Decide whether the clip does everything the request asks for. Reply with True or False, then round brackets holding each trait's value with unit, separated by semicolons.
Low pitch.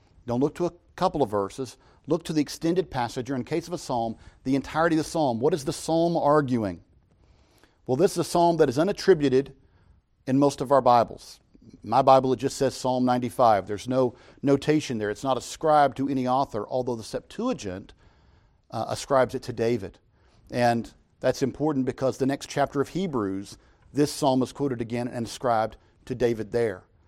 True (130 Hz)